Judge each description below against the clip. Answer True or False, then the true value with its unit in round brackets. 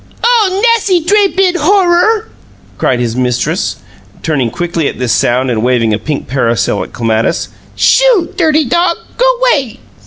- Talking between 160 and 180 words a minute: False (150 wpm)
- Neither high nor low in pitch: False (270 Hz)